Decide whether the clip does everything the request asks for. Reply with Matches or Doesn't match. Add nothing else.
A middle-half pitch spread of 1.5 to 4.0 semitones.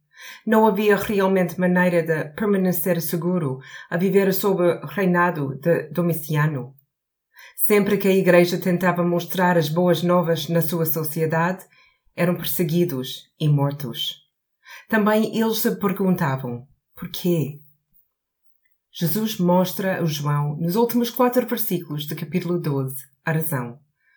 Matches